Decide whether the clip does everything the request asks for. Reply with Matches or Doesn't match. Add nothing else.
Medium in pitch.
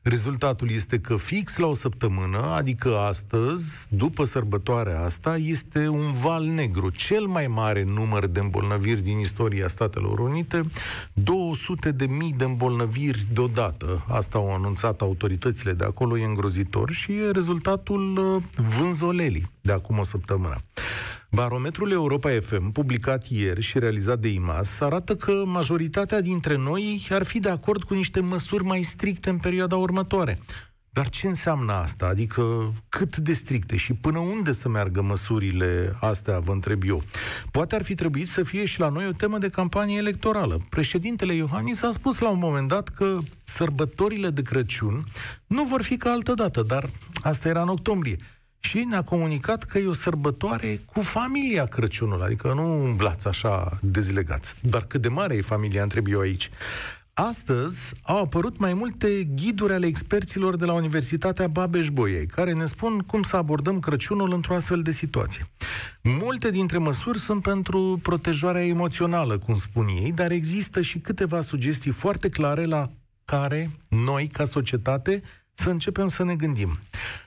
Matches